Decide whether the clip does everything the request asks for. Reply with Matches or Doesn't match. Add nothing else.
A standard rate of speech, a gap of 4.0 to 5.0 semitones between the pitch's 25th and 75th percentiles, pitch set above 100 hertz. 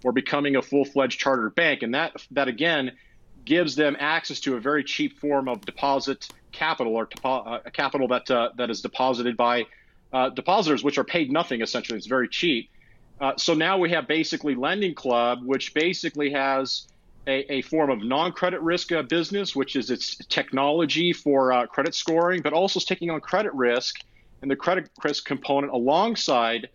Matches